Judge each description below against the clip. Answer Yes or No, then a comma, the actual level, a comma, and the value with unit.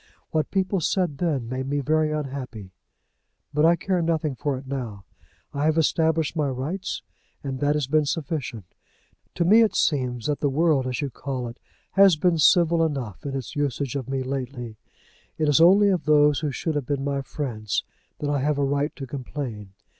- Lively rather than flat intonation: No, average, 3.2 semitones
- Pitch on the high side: No, medium, 145 Hz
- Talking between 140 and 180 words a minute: No, average, 190 wpm